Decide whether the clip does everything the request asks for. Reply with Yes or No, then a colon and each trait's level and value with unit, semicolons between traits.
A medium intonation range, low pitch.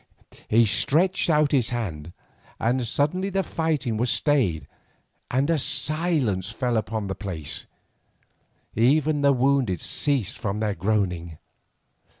No: wide, 6.2 semitones; low, 120 Hz